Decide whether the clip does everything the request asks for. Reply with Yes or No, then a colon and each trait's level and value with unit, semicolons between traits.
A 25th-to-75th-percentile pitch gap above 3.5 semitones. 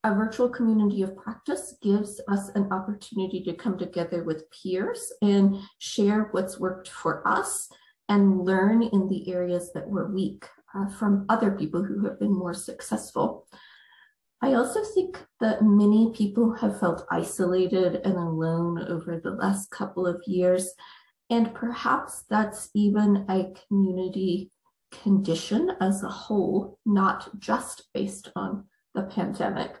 No: average, 2.8 semitones